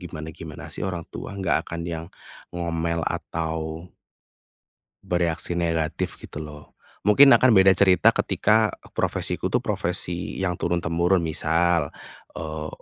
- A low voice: Yes, very low, 85 Hz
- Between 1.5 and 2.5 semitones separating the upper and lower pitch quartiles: Yes, narrow, 1.8 semitones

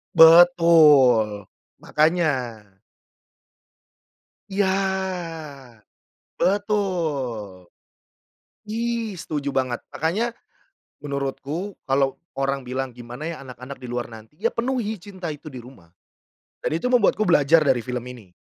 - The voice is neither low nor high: Yes, medium, 150 Hz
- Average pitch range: No, wide, 6.8 semitones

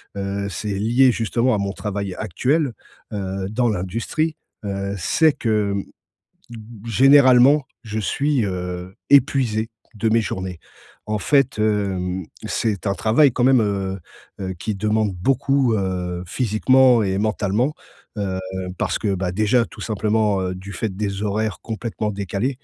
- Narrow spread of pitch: No, average, 3.6 semitones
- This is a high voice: No, low, 105 Hz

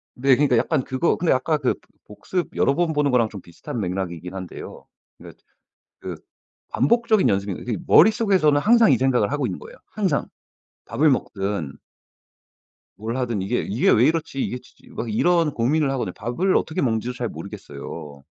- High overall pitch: No, low, 125 Hz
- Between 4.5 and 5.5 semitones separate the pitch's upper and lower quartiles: No, wide, 7.2 semitones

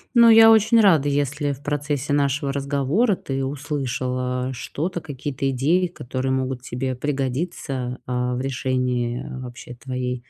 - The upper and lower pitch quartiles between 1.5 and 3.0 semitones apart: Yes, narrow, 2.5 semitones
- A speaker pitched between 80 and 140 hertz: Yes, low, 135 Hz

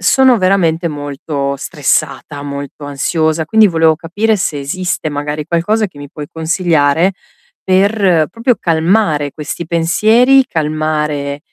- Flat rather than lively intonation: No, average, 4.2 semitones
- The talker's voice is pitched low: No, medium, 160 Hz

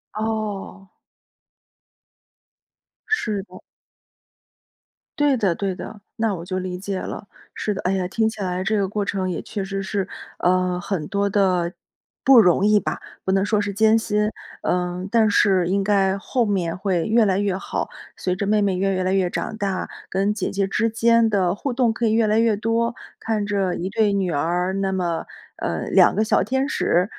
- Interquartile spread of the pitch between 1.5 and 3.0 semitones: Yes, narrow, 2.6 semitones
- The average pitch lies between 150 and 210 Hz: Yes, high, 200 Hz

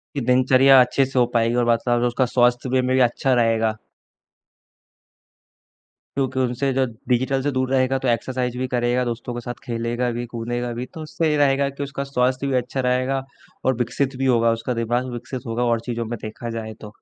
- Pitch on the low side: Yes, low, 125 Hz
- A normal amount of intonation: No, narrow, 1.7 semitones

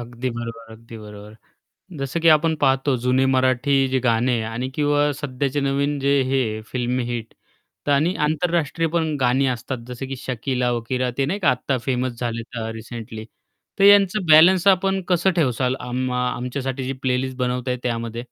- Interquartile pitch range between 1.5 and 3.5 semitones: Yes, average, 3.0 semitones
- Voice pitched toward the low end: Yes, low, 130 Hz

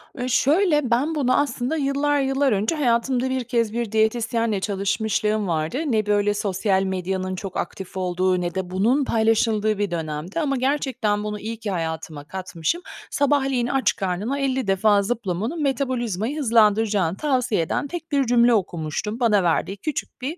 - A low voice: No, high, 220 Hz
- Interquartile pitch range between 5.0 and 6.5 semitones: Yes, wide, 5.4 semitones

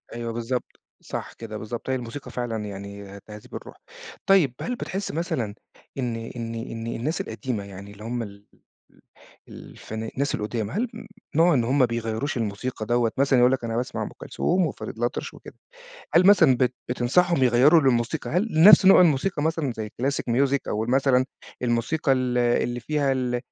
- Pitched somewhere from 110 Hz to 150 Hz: Yes, low, 125 Hz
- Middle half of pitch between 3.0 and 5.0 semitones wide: Yes, average, 3.7 semitones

